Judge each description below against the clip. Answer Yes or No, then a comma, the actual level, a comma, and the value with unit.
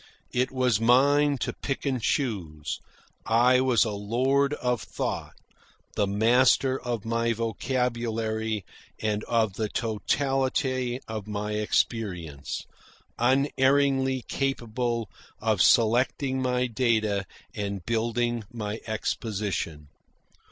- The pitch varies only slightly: No, average, 3.3 semitones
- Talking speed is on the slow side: Yes, slow, 100 wpm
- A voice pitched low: Yes, low, 115 Hz